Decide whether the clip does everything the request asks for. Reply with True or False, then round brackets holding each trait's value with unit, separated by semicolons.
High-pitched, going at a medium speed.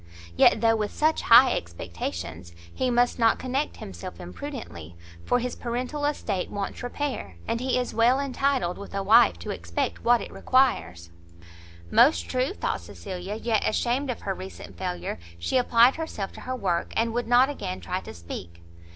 True (230 Hz; 170 wpm)